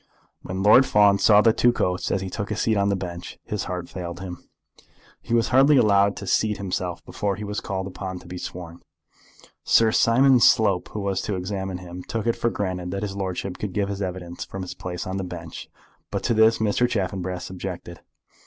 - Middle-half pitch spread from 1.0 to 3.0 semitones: Yes, narrow, 2.6 semitones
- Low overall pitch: Yes, very low, 95 Hz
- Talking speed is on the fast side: Yes, fast, 210 wpm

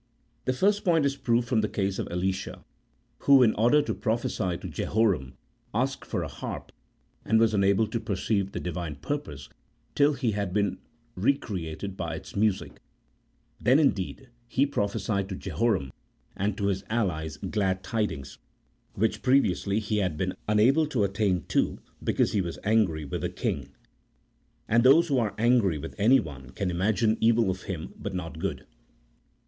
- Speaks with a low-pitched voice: Yes, low, 105 Hz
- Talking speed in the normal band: Yes, average, 165 wpm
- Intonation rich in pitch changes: No, average, 4.2 semitones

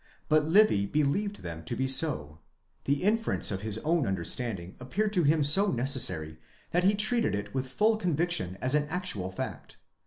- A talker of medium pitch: Yes, medium, 145 Hz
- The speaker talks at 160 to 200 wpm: Yes, average, 180 wpm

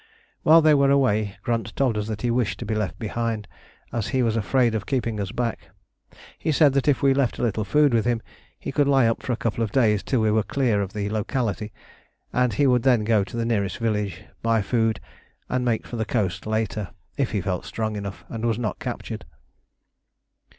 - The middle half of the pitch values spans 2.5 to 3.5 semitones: Yes, average, 2.9 semitones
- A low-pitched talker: Yes, low, 115 Hz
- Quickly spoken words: Yes, fast, 220 wpm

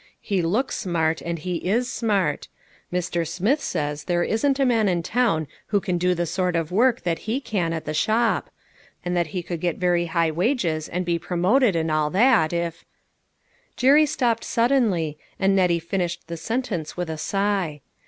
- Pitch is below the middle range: No, medium, 180 Hz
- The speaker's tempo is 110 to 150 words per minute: No, average, 185 wpm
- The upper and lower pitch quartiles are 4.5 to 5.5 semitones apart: Yes, average, 4.9 semitones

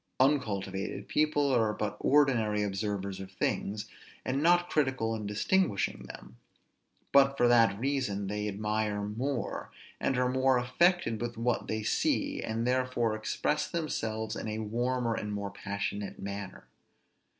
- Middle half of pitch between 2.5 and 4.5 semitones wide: Yes, average, 4.1 semitones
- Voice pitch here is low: Yes, low, 110 Hz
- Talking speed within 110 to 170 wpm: Yes, average, 140 wpm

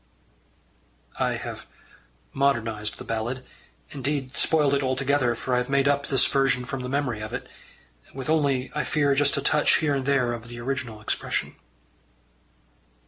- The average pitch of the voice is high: No, low, 135 Hz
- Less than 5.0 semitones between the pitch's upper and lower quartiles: Yes, narrow, 2.4 semitones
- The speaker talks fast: No, average, 160 wpm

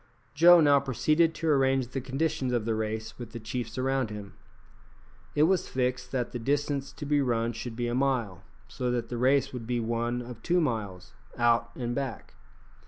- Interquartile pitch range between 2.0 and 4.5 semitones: Yes, average, 2.9 semitones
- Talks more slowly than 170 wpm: No, average, 190 wpm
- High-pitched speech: No, low, 125 Hz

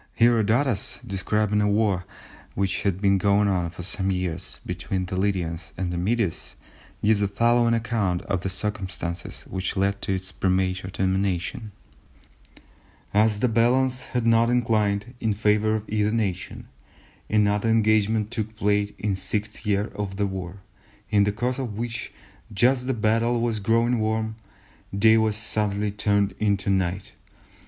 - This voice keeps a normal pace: Yes, average, 150 wpm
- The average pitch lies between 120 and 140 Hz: No, low, 105 Hz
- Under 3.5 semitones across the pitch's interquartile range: Yes, narrow, 2.6 semitones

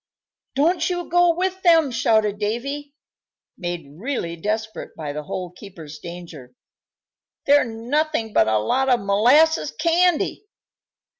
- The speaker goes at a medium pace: No, slow, 125 wpm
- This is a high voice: Yes, high, 230 Hz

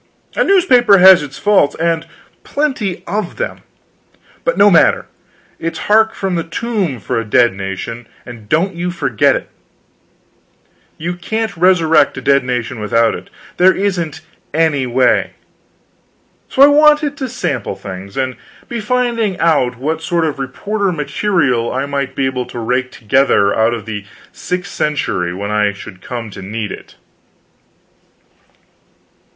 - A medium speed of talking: Yes, average, 145 wpm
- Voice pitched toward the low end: No, medium, 155 Hz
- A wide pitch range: Yes, wide, 8.6 semitones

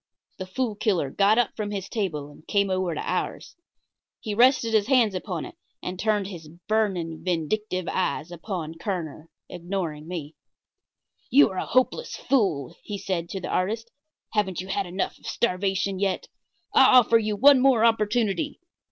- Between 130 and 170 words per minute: Yes, average, 165 wpm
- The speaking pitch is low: No, high, 195 Hz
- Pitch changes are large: No, average, 3.8 semitones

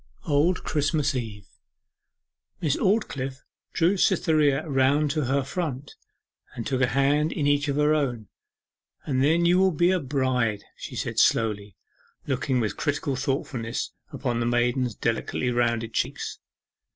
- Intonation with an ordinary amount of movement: Yes, average, 3.6 semitones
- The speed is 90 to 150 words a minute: Yes, average, 140 wpm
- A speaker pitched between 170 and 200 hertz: No, low, 135 Hz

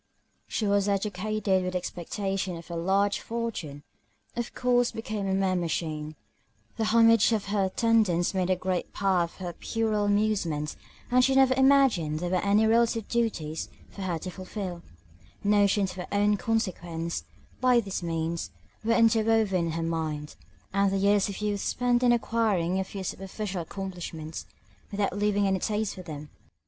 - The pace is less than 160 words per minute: No, average, 165 wpm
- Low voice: No, high, 195 Hz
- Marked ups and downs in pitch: No, average, 3.8 semitones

